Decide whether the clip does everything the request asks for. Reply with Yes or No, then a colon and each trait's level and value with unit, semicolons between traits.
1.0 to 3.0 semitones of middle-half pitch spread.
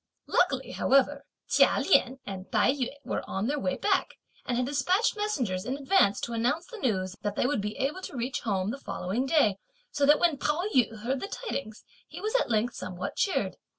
No: wide, 5.6 semitones